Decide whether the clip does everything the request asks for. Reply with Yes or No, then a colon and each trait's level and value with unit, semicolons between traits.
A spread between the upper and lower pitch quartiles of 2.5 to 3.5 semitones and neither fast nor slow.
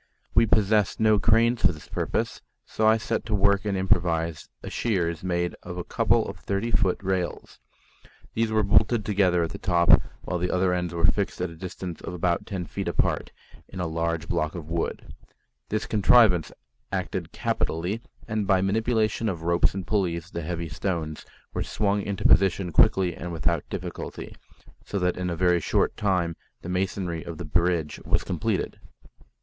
Yes: average, 3.0 semitones; average, 175 wpm